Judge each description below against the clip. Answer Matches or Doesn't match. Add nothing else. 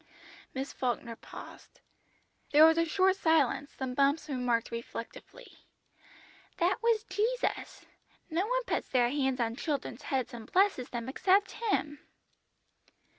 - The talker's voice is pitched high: Matches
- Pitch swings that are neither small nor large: Doesn't match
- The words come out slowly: Matches